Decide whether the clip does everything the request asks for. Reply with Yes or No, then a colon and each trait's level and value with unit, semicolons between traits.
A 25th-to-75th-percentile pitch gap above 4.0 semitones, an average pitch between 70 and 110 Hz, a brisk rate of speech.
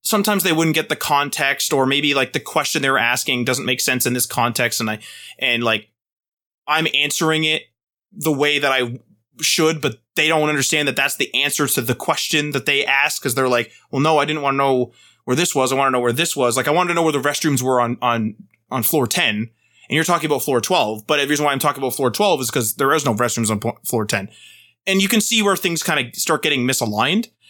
No: average, 4.4 semitones; low, 135 Hz; fast, 250 wpm